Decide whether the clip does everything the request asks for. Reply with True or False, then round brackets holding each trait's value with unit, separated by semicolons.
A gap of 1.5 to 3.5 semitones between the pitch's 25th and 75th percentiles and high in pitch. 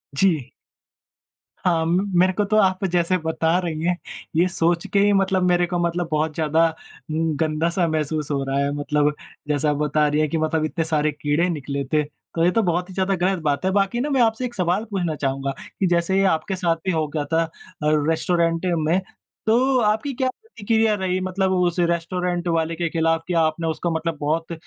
False (3.0 semitones; 170 Hz)